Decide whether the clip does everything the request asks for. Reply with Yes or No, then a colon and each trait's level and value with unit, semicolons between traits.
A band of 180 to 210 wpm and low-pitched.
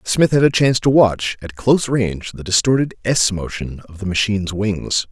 Yes: average, 200 wpm; low, 105 Hz